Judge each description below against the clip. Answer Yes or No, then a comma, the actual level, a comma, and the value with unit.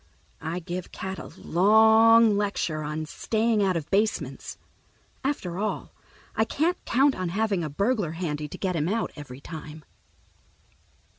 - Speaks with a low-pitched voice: No, high, 190 Hz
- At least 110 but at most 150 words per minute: Yes, average, 145 wpm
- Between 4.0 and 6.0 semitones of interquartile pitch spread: Yes, wide, 5.4 semitones